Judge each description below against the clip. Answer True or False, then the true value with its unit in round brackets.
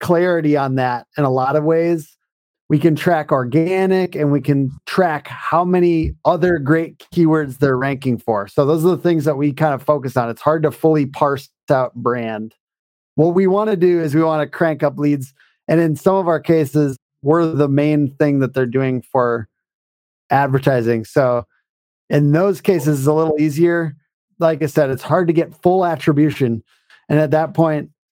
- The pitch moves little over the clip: False (3.3 semitones)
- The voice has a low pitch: False (150 Hz)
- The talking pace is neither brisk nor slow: True (190 wpm)